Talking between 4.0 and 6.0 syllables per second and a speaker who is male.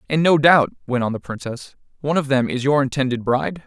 No: 6.2 syllables/s; male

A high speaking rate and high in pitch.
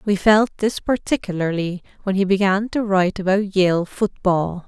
No: average, 155 wpm; high, 195 Hz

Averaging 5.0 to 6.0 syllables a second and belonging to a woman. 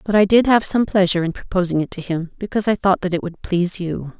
No: 6.5 syllables/s; female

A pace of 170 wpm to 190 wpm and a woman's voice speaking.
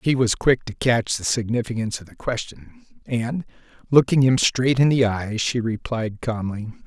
No: average, 175 wpm; male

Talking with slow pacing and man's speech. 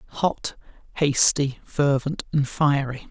Yes: slow, 95 wpm; male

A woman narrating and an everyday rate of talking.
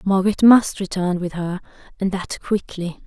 Yes: female; average, 155 wpm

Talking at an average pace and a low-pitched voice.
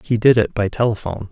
No: fast, 225 wpm; low, 105 Hz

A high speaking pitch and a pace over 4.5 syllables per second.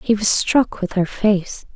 No: high, 205 Hz; 3.8 syllables/s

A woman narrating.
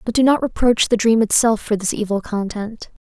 Yes: female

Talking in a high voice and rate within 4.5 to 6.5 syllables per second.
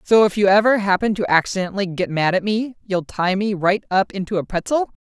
Yes: high, 200 Hz; 5.8 syllables/s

